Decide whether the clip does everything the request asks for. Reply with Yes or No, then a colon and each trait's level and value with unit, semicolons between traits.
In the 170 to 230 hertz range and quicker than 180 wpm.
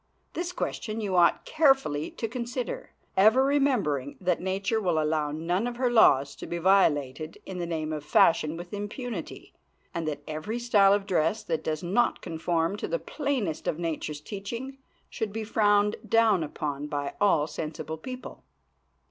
No: high, 190 Hz; average, 165 wpm